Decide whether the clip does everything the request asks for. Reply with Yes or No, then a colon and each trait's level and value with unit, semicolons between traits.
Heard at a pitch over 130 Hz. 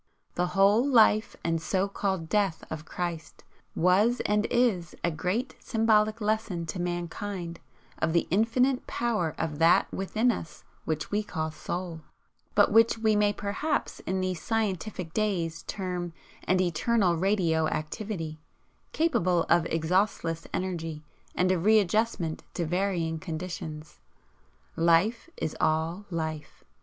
Yes: medium, 185 Hz